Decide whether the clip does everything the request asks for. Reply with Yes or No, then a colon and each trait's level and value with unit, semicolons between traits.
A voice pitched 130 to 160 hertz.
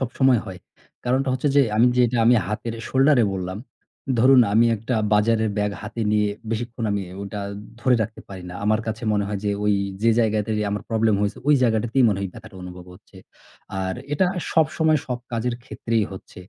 No: low, 110 Hz